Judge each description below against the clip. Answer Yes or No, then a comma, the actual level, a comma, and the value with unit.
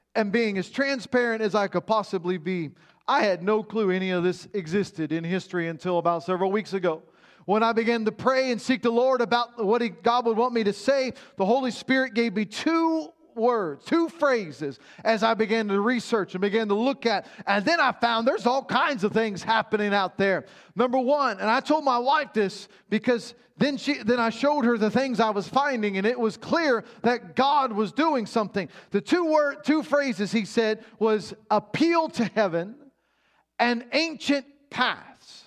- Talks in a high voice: Yes, high, 225 Hz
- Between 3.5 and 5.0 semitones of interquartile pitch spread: Yes, average, 4.4 semitones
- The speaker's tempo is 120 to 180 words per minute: No, average, 195 wpm